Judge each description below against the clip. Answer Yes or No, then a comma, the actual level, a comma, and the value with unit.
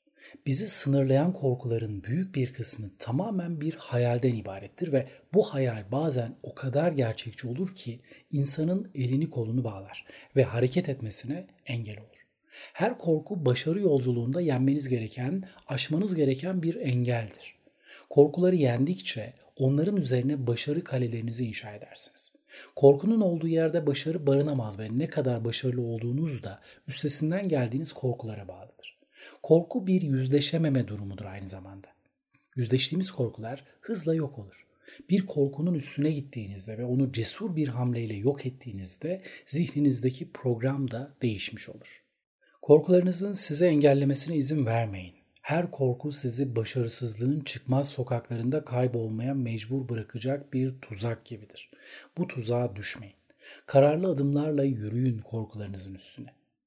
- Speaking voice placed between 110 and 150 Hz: Yes, low, 135 Hz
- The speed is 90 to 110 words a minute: No, average, 120 wpm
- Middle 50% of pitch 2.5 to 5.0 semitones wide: Yes, average, 4.5 semitones